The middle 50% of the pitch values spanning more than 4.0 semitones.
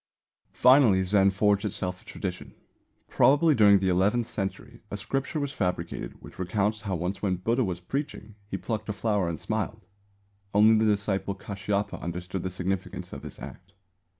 No: average, 2.9 semitones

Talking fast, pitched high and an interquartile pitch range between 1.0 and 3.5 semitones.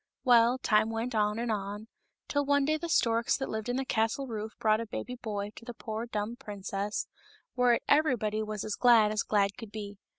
Yes: fast, 210 wpm; high, 225 Hz; narrow, 2.6 semitones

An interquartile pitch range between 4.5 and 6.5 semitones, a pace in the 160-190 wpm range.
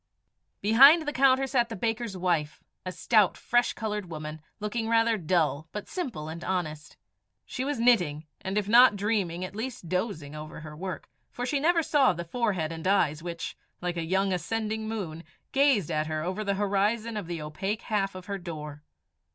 Yes: wide, 5.5 semitones; average, 185 wpm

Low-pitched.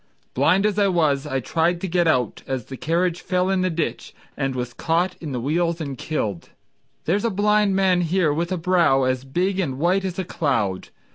No: medium, 170 Hz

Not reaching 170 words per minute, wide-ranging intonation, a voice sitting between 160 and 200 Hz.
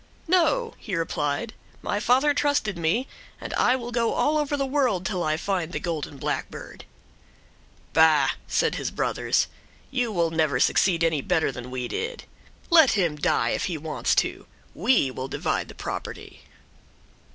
Yes: average, 160 wpm; wide, 8.6 semitones; high, 190 Hz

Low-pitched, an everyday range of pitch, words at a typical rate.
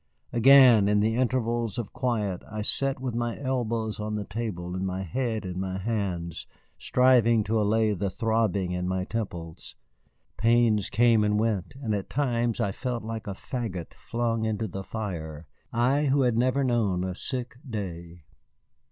Yes: low, 110 Hz; average, 3.7 semitones; average, 165 wpm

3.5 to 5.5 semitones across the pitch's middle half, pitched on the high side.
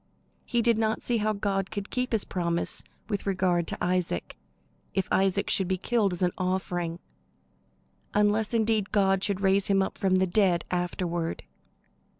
No: narrow, 2.5 semitones; high, 195 Hz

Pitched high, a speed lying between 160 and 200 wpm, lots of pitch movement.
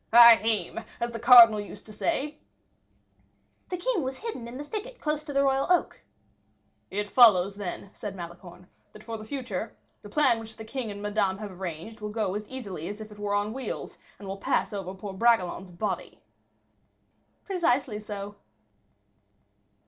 No: high, 215 Hz; average, 170 wpm; average, 4.2 semitones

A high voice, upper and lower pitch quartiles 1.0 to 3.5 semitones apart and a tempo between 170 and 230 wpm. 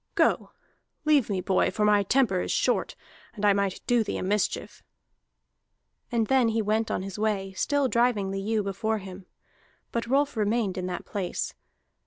Yes: high, 210 Hz; average, 3.1 semitones; average, 175 wpm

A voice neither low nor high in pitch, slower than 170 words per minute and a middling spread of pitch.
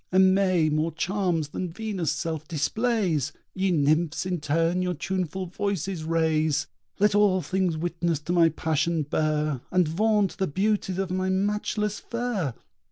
Yes: medium, 175 Hz; average, 145 wpm; average, 3.4 semitones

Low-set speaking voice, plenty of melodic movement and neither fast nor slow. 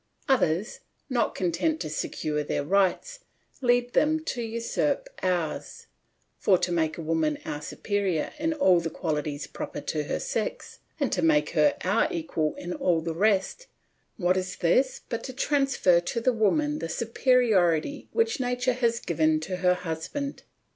No: medium, 185 Hz; wide, 7.3 semitones; average, 155 wpm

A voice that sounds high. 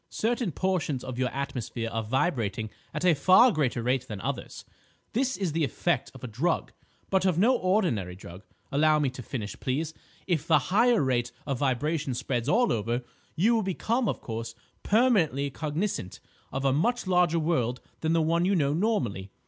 No: medium, 150 Hz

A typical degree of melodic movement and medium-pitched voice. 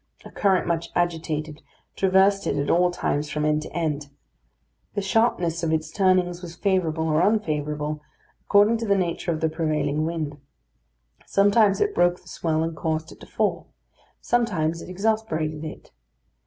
Yes: average, 3.7 semitones; medium, 170 Hz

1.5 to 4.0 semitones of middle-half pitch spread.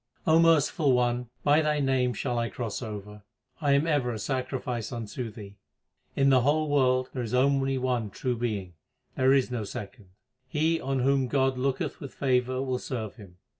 Yes: narrow, 2.6 semitones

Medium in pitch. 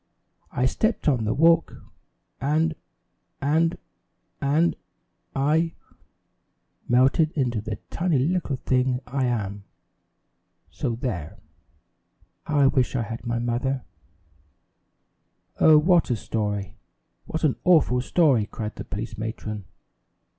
No: low, 130 Hz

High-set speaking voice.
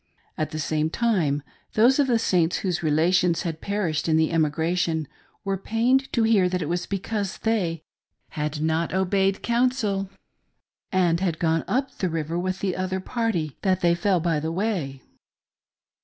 No: medium, 180 Hz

